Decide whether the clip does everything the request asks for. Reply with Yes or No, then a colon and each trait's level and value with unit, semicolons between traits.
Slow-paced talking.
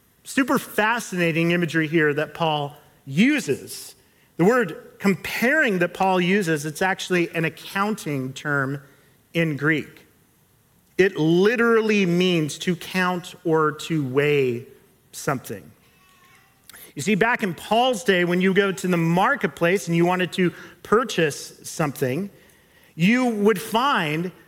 Yes: slow, 125 wpm